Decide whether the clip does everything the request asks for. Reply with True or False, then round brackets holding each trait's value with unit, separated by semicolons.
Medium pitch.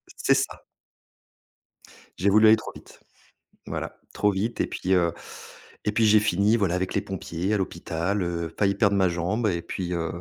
False (95 Hz)